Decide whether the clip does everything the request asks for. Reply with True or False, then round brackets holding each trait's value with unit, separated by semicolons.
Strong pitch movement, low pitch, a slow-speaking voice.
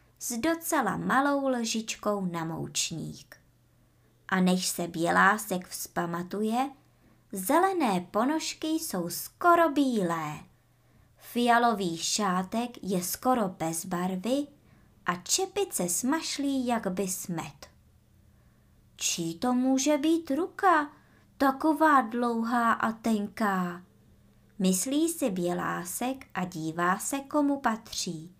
False (7.6 semitones; 215 Hz; 95 wpm)